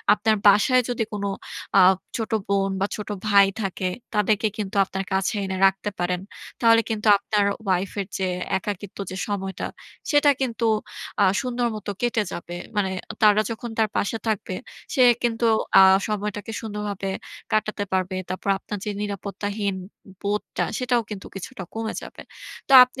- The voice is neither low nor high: No, high, 205 Hz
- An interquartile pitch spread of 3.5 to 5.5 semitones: No, narrow, 2.4 semitones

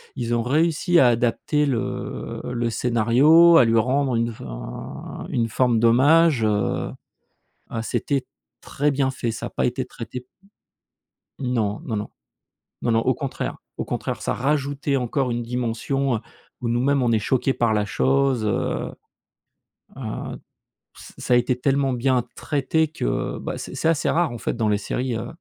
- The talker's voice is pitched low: Yes, low, 125 Hz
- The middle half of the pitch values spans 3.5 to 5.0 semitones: No, average, 3.0 semitones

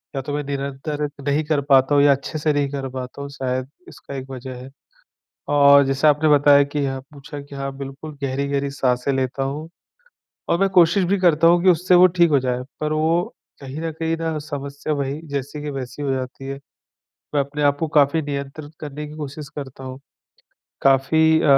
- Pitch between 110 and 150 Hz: Yes, medium, 140 Hz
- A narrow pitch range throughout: Yes, narrow, 2.1 semitones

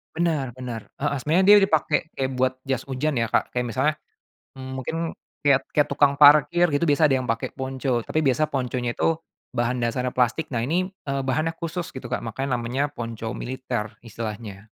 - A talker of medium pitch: No, low, 130 Hz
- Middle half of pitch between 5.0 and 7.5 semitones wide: No, average, 3.5 semitones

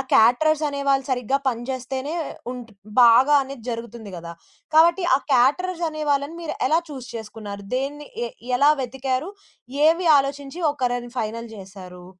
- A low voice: No, very high, 260 Hz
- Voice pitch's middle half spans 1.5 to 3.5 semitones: No, average, 3.9 semitones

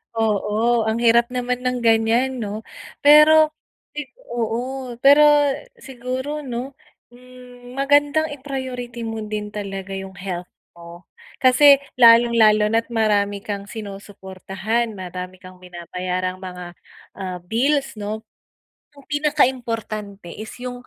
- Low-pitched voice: No, high, 225 Hz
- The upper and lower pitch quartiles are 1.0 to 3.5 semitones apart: No, average, 4.2 semitones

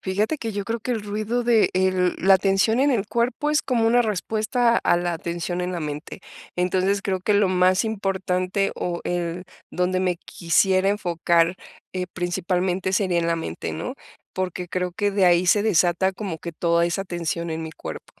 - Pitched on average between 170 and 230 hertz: Yes, medium, 185 Hz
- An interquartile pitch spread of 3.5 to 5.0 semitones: No, average, 2.9 semitones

